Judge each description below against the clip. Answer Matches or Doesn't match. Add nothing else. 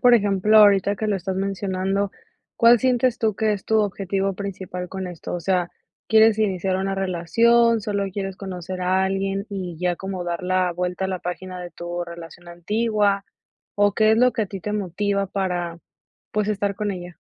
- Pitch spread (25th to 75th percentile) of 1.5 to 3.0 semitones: Matches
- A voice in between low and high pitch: Doesn't match